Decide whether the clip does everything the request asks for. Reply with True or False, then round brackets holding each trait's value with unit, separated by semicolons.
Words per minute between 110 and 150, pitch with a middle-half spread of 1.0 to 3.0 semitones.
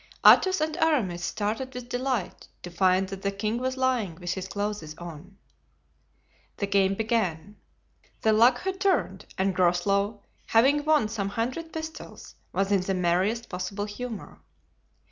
False (145 wpm; 4.8 semitones)